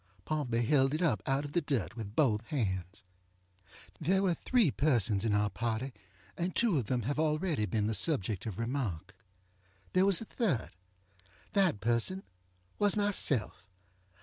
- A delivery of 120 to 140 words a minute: No, average, 150 wpm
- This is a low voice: Yes, low, 125 Hz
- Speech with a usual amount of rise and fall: No, wide, 7.3 semitones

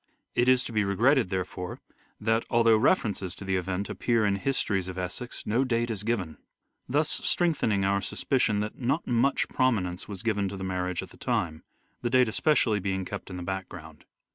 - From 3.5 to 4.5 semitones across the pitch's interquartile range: Yes, average, 4.1 semitones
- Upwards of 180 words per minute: Yes, average, 190 wpm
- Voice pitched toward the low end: Yes, low, 105 Hz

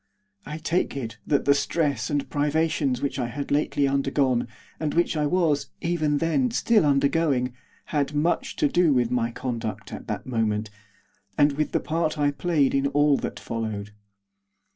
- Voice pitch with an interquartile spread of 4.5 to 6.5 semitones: No, average, 3.5 semitones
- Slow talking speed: No, average, 165 wpm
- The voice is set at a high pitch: No, medium, 145 Hz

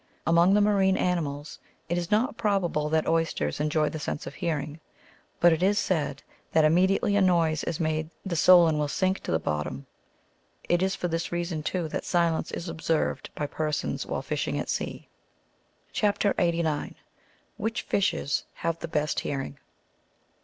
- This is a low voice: No, medium, 165 Hz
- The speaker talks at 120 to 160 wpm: No, average, 170 wpm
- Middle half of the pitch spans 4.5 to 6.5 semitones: No, average, 3.2 semitones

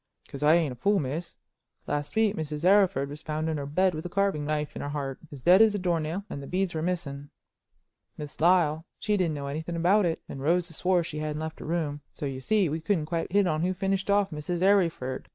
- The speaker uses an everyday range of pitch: Yes, average, 3.8 semitones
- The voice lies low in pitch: No, medium, 160 Hz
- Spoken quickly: Yes, fast, 240 wpm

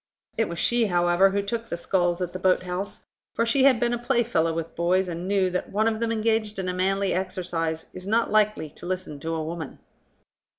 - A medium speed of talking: No, fast, 220 wpm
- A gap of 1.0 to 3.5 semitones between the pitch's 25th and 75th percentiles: No, average, 4.0 semitones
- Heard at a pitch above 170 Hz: Yes, medium, 185 Hz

